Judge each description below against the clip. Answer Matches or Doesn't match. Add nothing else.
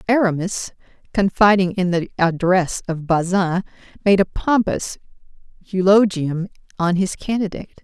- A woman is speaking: Matches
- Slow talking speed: Matches